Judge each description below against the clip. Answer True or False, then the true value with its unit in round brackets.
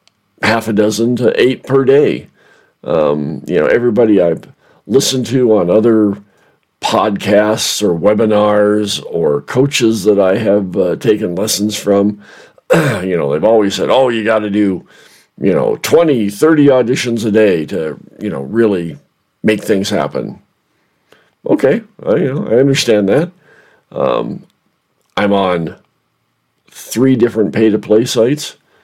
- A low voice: True (110 Hz)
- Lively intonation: False (2.5 semitones)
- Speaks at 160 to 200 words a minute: False (135 wpm)